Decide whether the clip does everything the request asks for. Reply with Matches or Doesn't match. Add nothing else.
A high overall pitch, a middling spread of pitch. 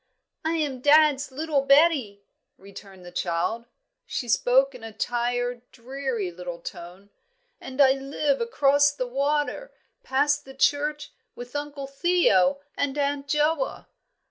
Matches